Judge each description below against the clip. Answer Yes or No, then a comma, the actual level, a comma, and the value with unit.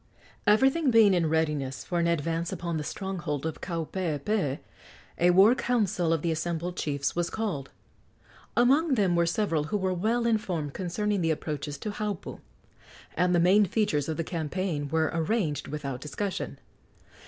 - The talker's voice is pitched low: No, medium, 170 Hz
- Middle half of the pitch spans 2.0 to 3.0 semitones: No, average, 4.8 semitones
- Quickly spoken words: No, average, 155 wpm